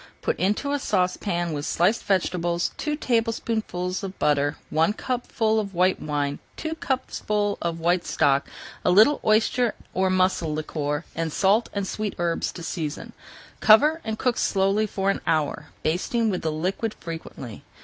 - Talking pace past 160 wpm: No, average, 155 wpm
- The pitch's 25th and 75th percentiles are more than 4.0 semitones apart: Yes, average, 4.8 semitones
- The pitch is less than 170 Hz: No, medium, 185 Hz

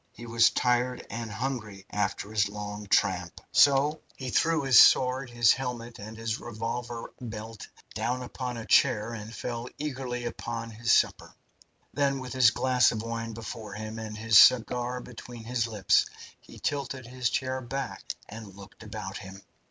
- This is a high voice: No, low, 115 Hz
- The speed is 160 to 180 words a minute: Yes, average, 165 wpm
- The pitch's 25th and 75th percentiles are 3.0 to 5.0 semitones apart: No, narrow, 2.6 semitones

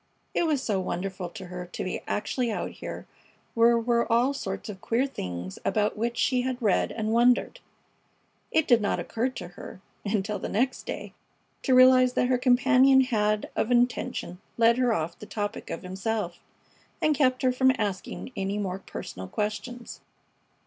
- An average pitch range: Yes, average, 4.4 semitones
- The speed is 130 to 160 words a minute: No, average, 170 wpm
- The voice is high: Yes, high, 230 Hz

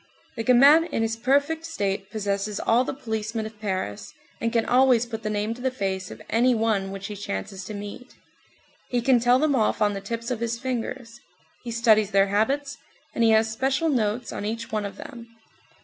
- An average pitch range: Yes, average, 3.2 semitones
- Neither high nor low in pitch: No, high, 225 Hz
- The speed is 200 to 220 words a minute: Yes, fast, 205 wpm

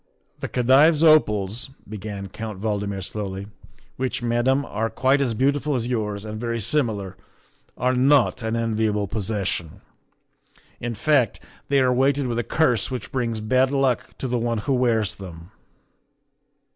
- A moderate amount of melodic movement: Yes, average, 3.8 semitones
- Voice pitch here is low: Yes, low, 115 Hz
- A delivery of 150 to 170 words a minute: Yes, average, 155 wpm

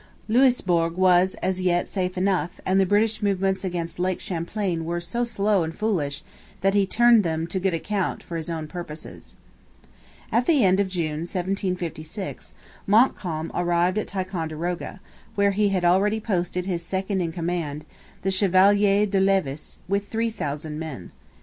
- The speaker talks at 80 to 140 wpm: No, average, 155 wpm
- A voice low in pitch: No, medium, 185 Hz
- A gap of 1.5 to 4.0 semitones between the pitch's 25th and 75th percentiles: Yes, average, 2.9 semitones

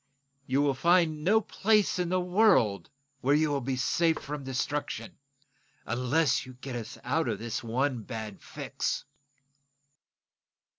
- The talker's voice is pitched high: No, medium, 140 Hz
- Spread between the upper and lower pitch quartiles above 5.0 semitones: Yes, wide, 5.4 semitones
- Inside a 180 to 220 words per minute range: No, average, 140 wpm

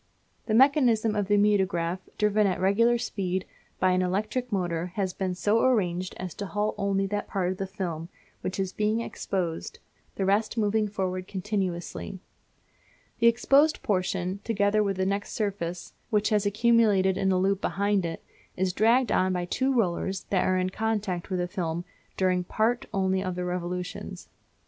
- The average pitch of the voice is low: No, high, 195 Hz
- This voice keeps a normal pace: Yes, average, 170 wpm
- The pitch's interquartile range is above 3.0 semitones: No, narrow, 2.6 semitones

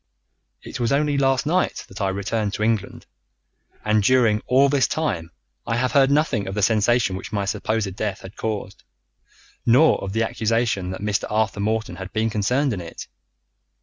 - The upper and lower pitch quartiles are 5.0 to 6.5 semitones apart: No, average, 4.1 semitones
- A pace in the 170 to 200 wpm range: Yes, average, 180 wpm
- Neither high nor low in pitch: No, low, 110 Hz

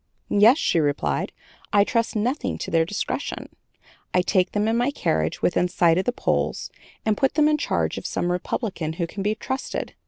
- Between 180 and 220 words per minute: Yes, average, 190 wpm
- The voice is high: Yes, high, 205 Hz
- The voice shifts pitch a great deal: Yes, wide, 5.8 semitones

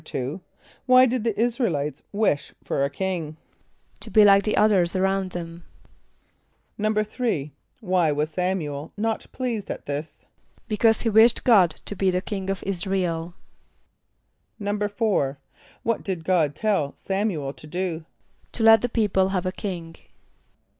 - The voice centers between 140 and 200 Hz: Yes, high, 190 Hz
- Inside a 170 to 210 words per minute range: No, average, 155 wpm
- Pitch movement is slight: No, average, 4.4 semitones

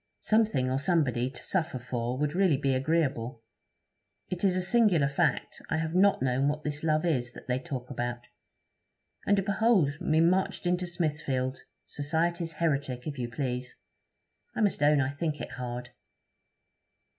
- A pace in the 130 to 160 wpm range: Yes, average, 155 wpm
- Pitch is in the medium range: Yes, medium, 145 Hz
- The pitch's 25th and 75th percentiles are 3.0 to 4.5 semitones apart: No, average, 5.0 semitones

